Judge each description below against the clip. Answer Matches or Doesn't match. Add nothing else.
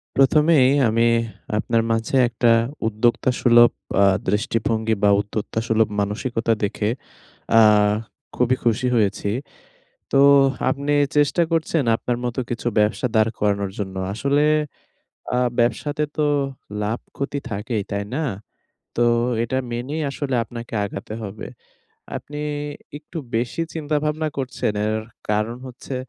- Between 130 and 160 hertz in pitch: Doesn't match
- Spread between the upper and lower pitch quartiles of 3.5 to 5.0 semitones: Matches